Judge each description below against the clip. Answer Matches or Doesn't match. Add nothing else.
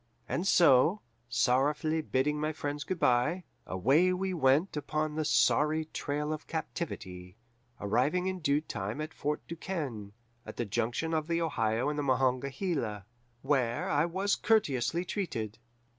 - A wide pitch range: Doesn't match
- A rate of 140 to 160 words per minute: Matches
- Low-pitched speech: Doesn't match